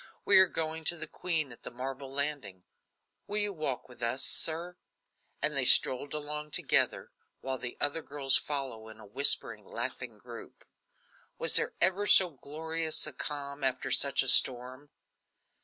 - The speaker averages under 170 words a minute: Yes, average, 160 wpm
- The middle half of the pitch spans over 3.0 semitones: Yes, average, 3.6 semitones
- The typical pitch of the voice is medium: Yes, medium, 145 Hz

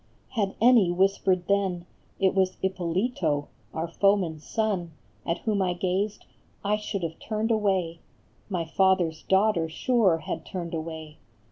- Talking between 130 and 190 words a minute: Yes, average, 145 wpm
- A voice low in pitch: No, medium, 185 Hz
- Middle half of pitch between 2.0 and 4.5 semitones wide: Yes, average, 3.2 semitones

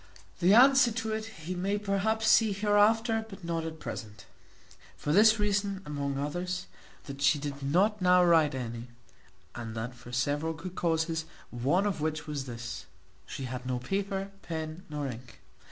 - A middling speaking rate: Yes, average, 165 wpm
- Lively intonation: Yes, wide, 6.4 semitones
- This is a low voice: No, medium, 165 Hz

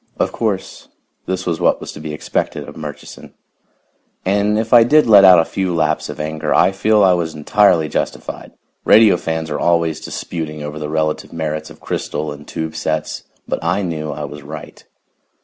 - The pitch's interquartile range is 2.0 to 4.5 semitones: Yes, average, 3.8 semitones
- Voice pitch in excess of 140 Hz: No, very low, 80 Hz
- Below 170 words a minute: No, average, 185 wpm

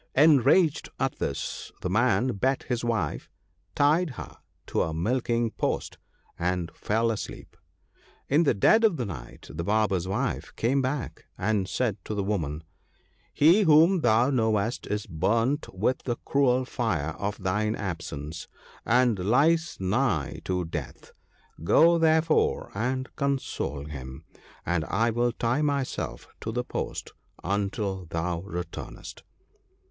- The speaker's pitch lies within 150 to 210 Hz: No, low, 115 Hz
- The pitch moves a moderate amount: No, wide, 6.3 semitones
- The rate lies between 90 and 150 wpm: Yes, slow, 135 wpm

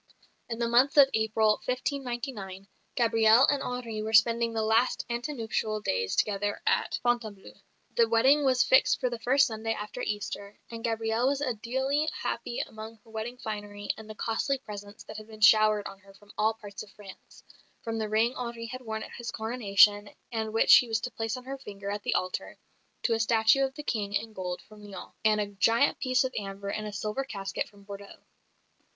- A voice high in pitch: Yes, high, 220 Hz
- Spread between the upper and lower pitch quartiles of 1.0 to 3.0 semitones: Yes, narrow, 2.6 semitones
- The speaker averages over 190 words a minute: Yes, average, 200 wpm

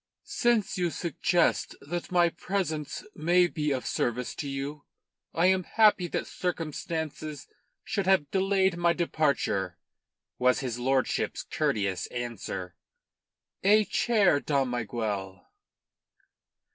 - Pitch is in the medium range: Yes, medium, 155 Hz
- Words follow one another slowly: Yes, slow, 110 wpm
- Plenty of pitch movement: Yes, wide, 6.0 semitones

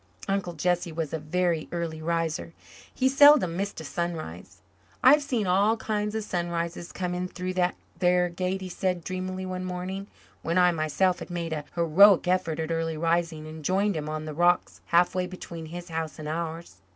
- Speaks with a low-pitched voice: No, medium, 175 Hz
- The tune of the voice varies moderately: No, narrow, 2.2 semitones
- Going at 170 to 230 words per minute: Yes, average, 185 wpm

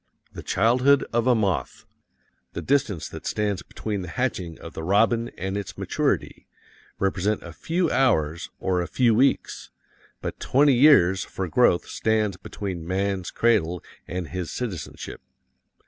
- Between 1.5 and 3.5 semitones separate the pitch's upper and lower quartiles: No, average, 5.0 semitones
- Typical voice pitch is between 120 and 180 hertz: No, low, 100 Hz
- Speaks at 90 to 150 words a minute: Yes, average, 145 wpm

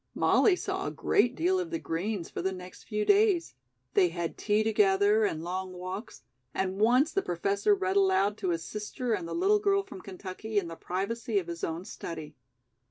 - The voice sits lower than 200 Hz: No, high, 205 Hz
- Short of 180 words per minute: No, average, 195 wpm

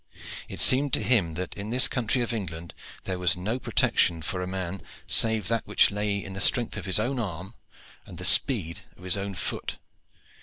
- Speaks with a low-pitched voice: Yes, low, 100 Hz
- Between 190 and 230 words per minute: Yes, average, 200 wpm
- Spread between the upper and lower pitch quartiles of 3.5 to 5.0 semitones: Yes, average, 4.0 semitones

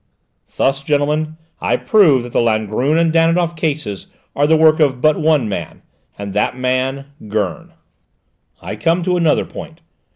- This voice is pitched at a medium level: Yes, medium, 145 Hz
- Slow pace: No, average, 155 wpm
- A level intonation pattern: No, average, 4.4 semitones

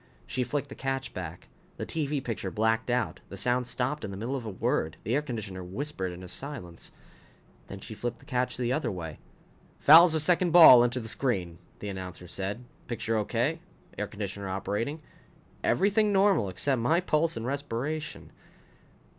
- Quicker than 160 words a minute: Yes, average, 175 wpm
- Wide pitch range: Yes, wide, 6.8 semitones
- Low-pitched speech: Yes, low, 120 Hz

